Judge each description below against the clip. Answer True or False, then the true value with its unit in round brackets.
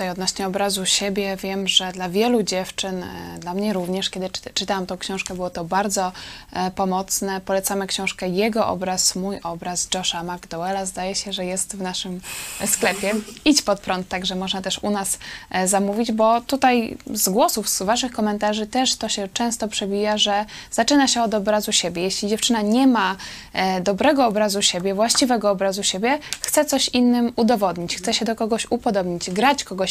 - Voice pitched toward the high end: True (200 Hz)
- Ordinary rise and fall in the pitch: True (3.2 semitones)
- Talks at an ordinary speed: False (165 wpm)